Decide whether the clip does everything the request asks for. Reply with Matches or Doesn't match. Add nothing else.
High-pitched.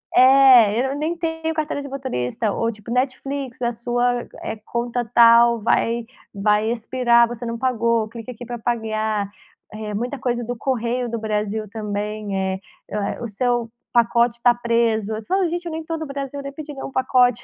Matches